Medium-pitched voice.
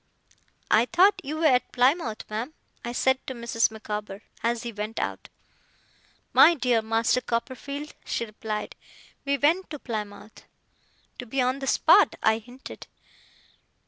No: high, 240 Hz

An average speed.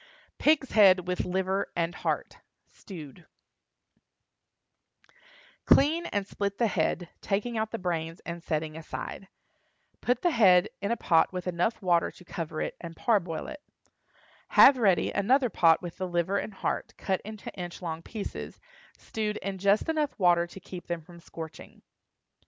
Yes: average, 155 wpm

